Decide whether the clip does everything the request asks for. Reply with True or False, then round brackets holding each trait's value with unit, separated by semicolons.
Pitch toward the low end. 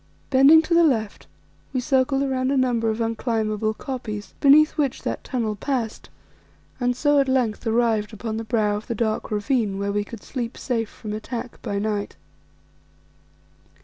False (230 Hz)